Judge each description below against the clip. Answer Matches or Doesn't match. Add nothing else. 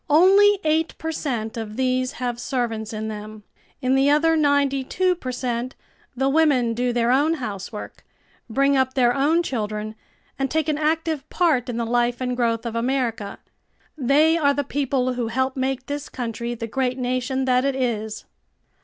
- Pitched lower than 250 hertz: Doesn't match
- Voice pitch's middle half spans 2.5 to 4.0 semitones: Matches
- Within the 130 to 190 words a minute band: Matches